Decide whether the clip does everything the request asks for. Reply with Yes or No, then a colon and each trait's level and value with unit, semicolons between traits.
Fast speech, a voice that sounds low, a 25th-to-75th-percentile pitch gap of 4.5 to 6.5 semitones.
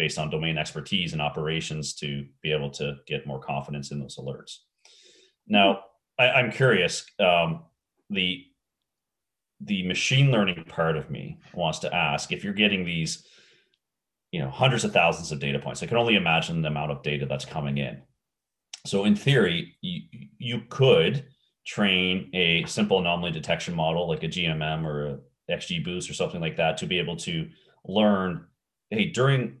No: average, 170 wpm; very low, 85 Hz; wide, 5.5 semitones